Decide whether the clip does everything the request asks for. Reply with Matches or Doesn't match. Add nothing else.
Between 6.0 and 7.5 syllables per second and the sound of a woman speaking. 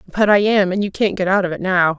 Matches